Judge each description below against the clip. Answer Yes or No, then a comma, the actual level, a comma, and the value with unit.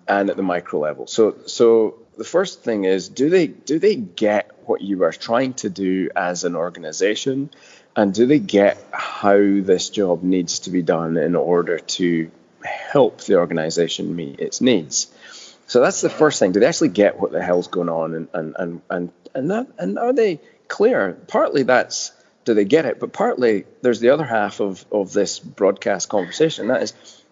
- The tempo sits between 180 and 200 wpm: Yes, average, 195 wpm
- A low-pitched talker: Yes, very low, 95 Hz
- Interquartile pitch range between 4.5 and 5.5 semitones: Yes, average, 4.8 semitones